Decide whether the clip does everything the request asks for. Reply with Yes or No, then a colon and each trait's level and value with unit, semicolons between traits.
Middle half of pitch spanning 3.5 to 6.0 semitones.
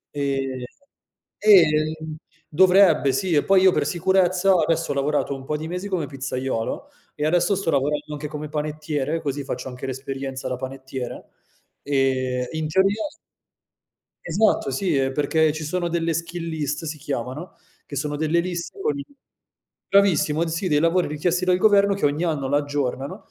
Yes: average, 4.3 semitones